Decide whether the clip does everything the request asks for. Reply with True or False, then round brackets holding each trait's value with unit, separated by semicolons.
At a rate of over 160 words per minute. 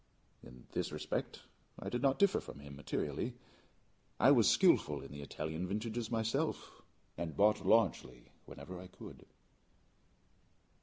False (135 wpm)